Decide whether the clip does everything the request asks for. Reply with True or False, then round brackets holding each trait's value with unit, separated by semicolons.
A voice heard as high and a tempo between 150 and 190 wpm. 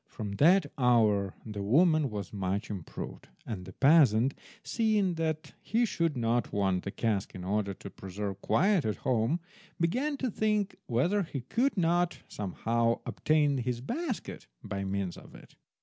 False (125 Hz; 155 wpm)